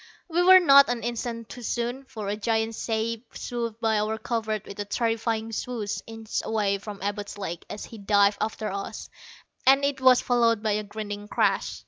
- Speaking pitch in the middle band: No, high, 225 Hz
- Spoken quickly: No, average, 185 wpm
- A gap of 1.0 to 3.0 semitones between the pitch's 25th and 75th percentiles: Yes, narrow, 2.4 semitones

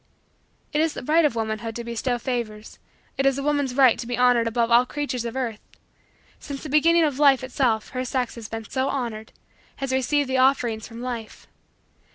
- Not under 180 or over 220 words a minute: Yes, average, 200 wpm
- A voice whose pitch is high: Yes, very high, 250 Hz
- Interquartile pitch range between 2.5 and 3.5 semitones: Yes, average, 2.9 semitones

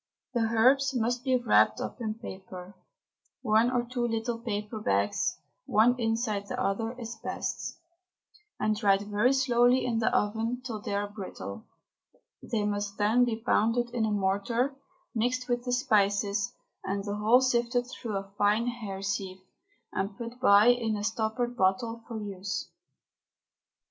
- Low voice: No, high, 225 Hz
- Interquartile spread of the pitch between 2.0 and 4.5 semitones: Yes, average, 3.0 semitones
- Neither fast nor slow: Yes, average, 155 wpm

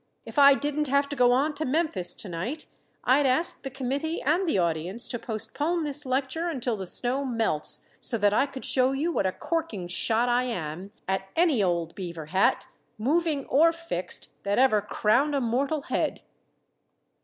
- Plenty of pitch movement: Yes, wide, 6.3 semitones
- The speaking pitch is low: No, very high, 255 Hz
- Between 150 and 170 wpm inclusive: No, average, 180 wpm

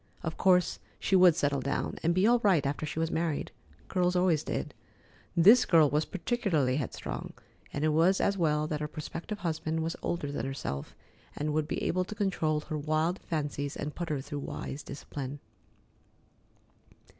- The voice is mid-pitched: Yes, medium, 155 Hz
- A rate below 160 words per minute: No, average, 175 wpm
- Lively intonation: No, average, 3.4 semitones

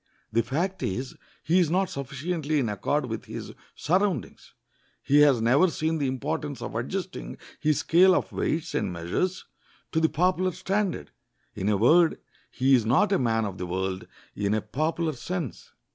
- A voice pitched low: No, medium, 150 Hz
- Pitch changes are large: Yes, wide, 7.1 semitones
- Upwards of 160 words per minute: Yes, average, 170 wpm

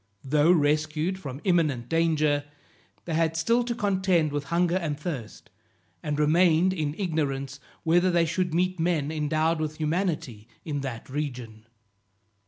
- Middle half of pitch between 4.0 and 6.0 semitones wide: No, average, 3.2 semitones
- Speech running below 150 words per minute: Yes, average, 140 wpm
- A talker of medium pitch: Yes, medium, 155 Hz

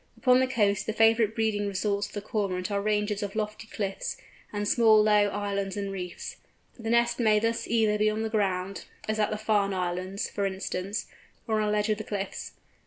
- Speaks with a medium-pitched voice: No, high, 210 Hz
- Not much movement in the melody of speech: Yes, narrow, 1.6 semitones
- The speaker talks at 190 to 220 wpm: Yes, average, 195 wpm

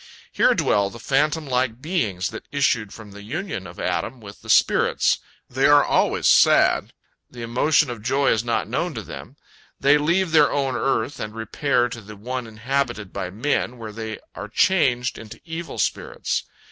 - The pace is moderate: Yes, average, 175 wpm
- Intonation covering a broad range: No, average, 4.8 semitones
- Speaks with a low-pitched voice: Yes, low, 125 Hz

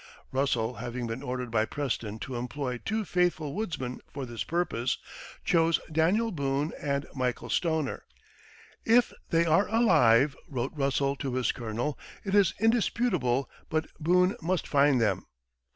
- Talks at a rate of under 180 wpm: Yes, average, 140 wpm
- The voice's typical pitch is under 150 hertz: Yes, medium, 140 Hz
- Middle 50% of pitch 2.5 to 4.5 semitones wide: No, wide, 5.5 semitones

